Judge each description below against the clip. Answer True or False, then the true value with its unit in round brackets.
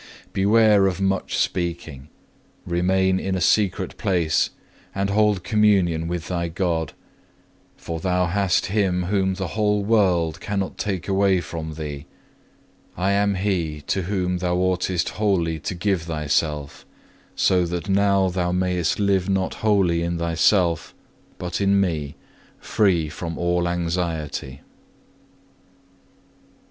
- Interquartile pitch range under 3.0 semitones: True (2.6 semitones)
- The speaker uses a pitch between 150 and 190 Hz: False (90 Hz)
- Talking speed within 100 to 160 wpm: True (135 wpm)